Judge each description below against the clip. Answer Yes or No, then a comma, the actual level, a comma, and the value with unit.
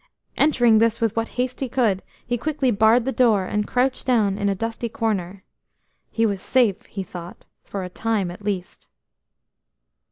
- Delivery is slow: No, average, 170 wpm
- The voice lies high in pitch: Yes, high, 225 Hz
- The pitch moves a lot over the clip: No, average, 3.6 semitones